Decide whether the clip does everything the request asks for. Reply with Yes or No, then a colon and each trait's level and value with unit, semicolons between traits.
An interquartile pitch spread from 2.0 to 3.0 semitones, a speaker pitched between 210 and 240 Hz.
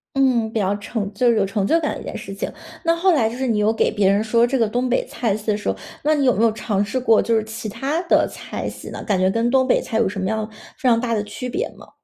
No: average, 3.4 semitones; high, 225 Hz